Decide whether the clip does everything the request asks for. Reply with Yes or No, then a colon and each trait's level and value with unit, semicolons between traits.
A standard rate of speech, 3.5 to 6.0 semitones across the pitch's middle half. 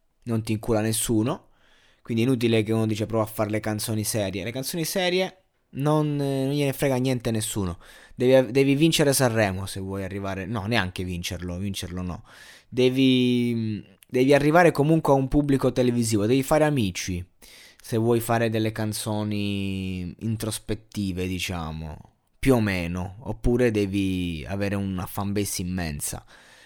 Yes: average, 145 wpm; average, 4.6 semitones